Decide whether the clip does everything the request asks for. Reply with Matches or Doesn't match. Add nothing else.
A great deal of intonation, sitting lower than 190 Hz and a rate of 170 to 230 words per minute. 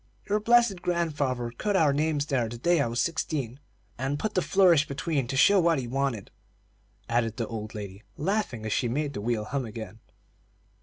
Matches